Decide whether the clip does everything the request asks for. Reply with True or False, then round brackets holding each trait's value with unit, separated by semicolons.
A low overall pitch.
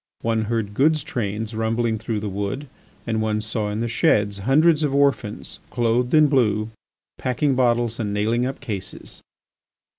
True (115 Hz)